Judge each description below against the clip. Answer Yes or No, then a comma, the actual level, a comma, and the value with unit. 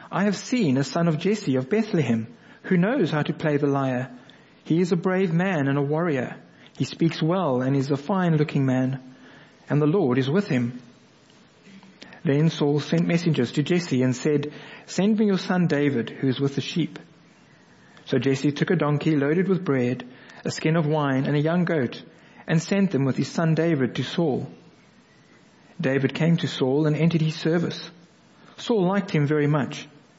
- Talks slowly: No, average, 190 wpm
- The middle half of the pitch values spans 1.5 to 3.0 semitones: No, average, 4.3 semitones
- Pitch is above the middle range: No, medium, 155 Hz